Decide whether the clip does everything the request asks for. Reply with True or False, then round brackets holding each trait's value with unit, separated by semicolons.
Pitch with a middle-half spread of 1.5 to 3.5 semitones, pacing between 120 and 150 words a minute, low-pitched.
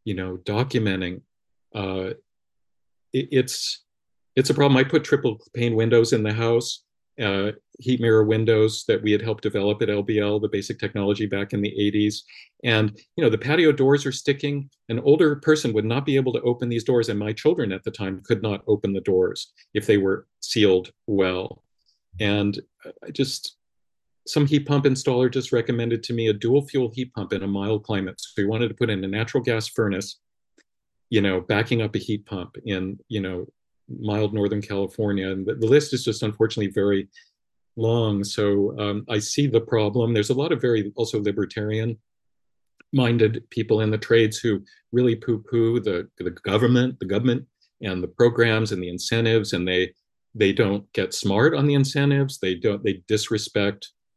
False (2.9 semitones; 185 wpm; 110 Hz)